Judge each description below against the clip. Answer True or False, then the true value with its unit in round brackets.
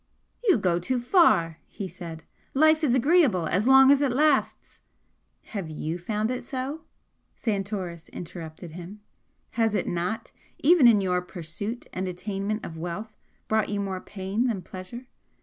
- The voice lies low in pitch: False (205 Hz)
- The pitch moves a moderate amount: False (5.8 semitones)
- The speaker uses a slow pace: False (155 wpm)